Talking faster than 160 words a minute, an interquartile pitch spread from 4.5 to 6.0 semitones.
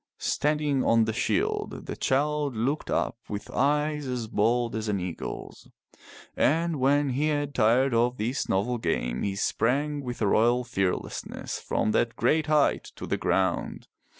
No: average, 155 wpm; average, 4.8 semitones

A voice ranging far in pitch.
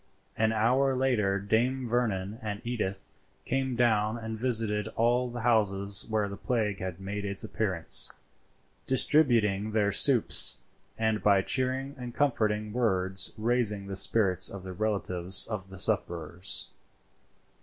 No: average, 3.6 semitones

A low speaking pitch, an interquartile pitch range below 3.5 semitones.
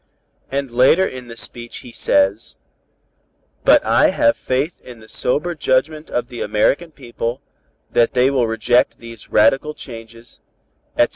Yes: low, 125 Hz; average, 2.9 semitones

